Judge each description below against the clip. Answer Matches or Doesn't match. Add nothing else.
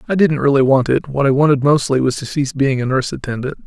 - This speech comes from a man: Matches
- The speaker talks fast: Matches